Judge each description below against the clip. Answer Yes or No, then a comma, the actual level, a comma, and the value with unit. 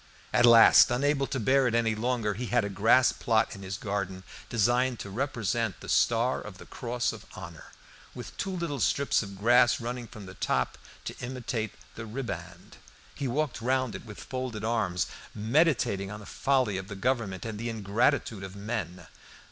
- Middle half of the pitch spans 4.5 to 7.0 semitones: No, average, 3.8 semitones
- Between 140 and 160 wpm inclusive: No, average, 180 wpm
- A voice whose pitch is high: No, low, 115 Hz